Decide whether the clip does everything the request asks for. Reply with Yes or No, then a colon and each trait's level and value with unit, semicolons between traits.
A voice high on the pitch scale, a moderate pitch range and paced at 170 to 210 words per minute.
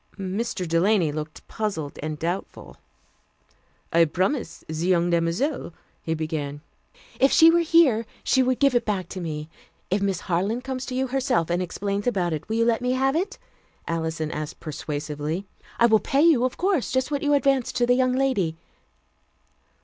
No: high, 200 Hz; wide, 7.8 semitones; average, 180 wpm